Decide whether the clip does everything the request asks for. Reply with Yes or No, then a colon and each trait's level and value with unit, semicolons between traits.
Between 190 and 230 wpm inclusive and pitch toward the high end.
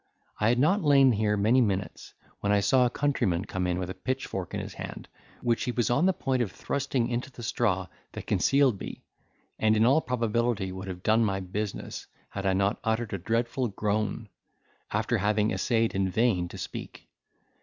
No: average, 195 wpm; low, 110 Hz